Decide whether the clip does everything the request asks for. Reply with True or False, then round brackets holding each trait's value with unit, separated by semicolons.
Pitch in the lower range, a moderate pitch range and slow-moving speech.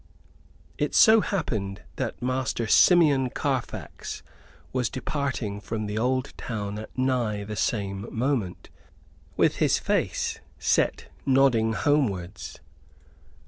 True (120 Hz; 4.2 semitones; 105 wpm)